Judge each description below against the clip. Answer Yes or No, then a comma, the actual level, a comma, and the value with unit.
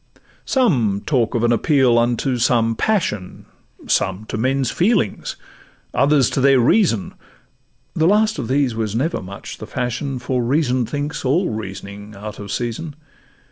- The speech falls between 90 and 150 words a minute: Yes, average, 145 wpm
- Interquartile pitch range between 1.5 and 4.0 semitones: No, average, 4.4 semitones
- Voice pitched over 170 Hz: No, low, 125 Hz